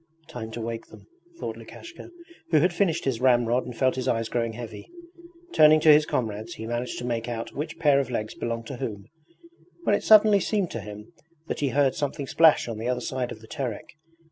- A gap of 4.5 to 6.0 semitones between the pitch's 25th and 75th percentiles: Yes, average, 4.8 semitones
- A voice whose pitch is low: Yes, low, 125 Hz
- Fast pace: Yes, fast, 215 wpm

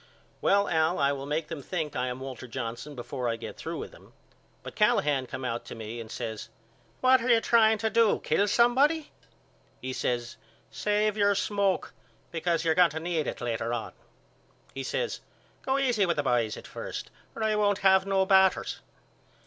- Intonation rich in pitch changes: Yes, wide, 8.2 semitones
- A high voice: No, medium, 170 Hz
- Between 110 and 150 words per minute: No, average, 190 wpm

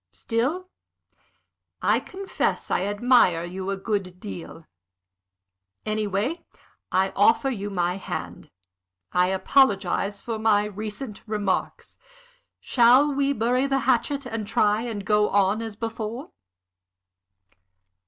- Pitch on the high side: Yes, high, 215 Hz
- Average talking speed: No, slow, 110 wpm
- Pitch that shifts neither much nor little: Yes, average, 3.7 semitones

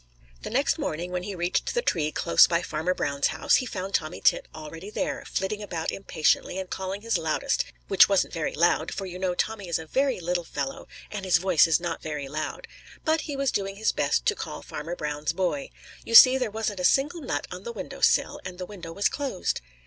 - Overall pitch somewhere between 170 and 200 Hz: Yes, medium, 185 Hz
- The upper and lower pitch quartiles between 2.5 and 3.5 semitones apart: No, average, 4.5 semitones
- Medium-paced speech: No, fast, 220 wpm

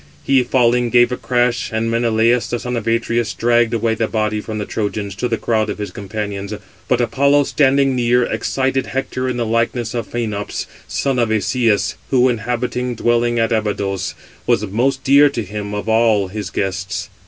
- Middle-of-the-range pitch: No, low, 115 Hz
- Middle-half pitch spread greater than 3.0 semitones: No, narrow, 2.5 semitones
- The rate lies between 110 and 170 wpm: No, average, 180 wpm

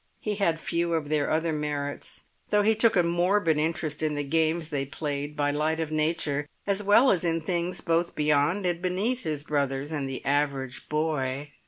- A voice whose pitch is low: No, medium, 155 Hz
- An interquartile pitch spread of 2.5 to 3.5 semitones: Yes, average, 2.9 semitones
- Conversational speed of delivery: Yes, average, 190 wpm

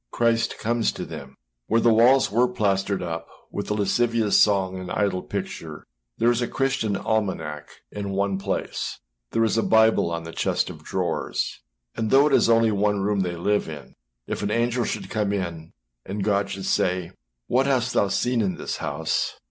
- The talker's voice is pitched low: Yes, low, 105 Hz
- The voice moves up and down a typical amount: Yes, average, 3.5 semitones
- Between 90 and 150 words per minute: No, average, 190 wpm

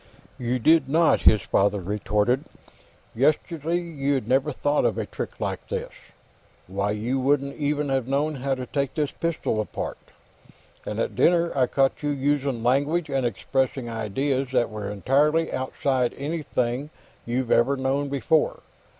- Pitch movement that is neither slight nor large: Yes, average, 3.2 semitones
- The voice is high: No, low, 135 Hz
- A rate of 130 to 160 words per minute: Yes, average, 150 wpm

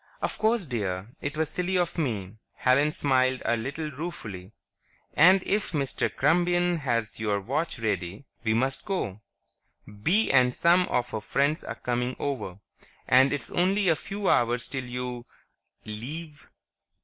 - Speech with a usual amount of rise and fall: No, wide, 6.2 semitones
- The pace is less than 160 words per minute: Yes, average, 150 wpm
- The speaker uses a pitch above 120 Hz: Yes, low, 135 Hz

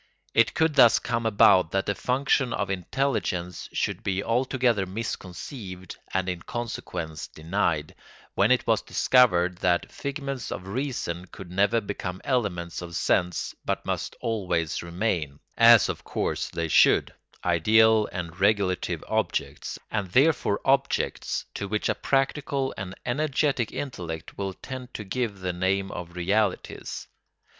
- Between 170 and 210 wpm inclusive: No, slow, 135 wpm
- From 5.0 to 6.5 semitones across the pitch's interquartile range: Yes, average, 5.3 semitones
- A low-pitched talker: Yes, low, 100 Hz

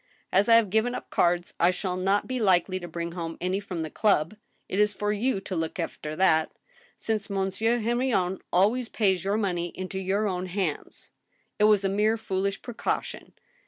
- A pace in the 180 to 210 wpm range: Yes, average, 195 wpm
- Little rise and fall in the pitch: No, average, 3.0 semitones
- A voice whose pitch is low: No, high, 195 Hz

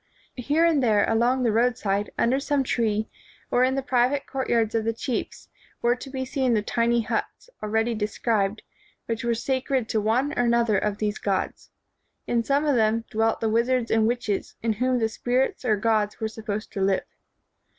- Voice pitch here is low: No, high, 230 Hz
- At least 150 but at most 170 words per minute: No, average, 185 wpm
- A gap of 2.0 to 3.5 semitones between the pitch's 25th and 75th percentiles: Yes, average, 2.7 semitones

